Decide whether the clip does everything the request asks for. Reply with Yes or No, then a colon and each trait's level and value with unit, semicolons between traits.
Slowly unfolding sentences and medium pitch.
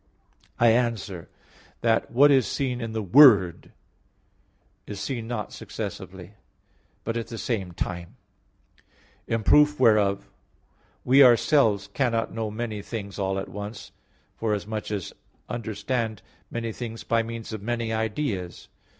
No: slow, 125 wpm; low, 110 Hz